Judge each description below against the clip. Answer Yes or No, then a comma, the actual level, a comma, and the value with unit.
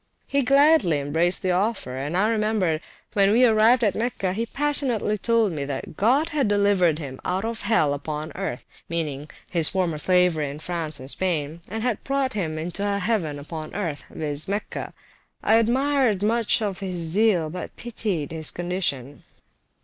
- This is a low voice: No, high, 190 Hz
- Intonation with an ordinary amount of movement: No, wide, 6.0 semitones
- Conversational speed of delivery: Yes, average, 165 wpm